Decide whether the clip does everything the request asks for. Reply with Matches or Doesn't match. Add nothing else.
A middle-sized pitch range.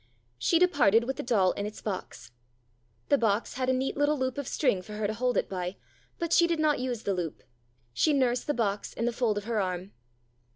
Matches